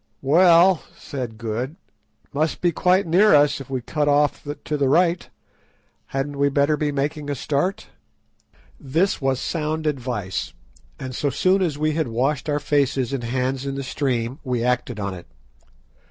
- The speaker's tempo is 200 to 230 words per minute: No, average, 170 wpm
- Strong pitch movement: No, average, 3.2 semitones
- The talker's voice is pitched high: No, medium, 140 Hz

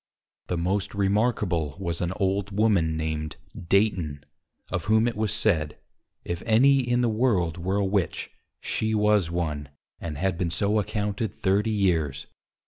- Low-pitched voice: Yes, very low, 95 Hz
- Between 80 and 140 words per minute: No, average, 150 wpm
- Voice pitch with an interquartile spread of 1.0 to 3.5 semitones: No, average, 4.2 semitones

